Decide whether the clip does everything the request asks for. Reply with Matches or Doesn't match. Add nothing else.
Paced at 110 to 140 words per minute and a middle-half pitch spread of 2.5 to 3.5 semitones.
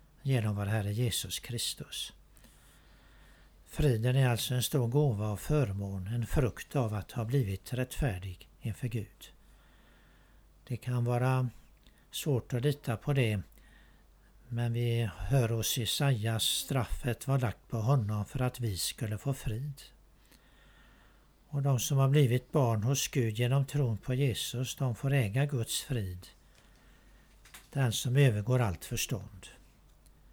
Doesn't match